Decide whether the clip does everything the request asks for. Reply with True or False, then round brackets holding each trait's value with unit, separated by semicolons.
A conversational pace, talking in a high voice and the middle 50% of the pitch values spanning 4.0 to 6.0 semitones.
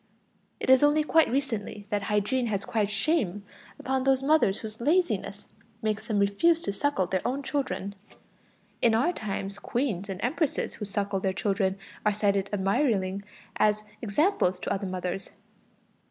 True (155 wpm; 210 Hz; 5.2 semitones)